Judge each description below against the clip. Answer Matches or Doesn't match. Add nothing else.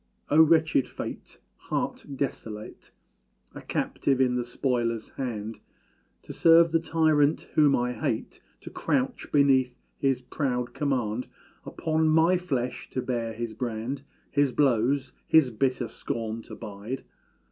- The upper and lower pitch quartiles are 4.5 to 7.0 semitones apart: Doesn't match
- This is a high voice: Doesn't match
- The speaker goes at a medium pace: Doesn't match